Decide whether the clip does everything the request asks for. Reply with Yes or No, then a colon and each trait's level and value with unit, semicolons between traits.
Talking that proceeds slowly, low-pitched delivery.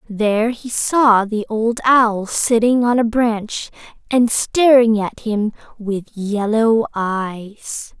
No: slow, 130 wpm; high, 225 Hz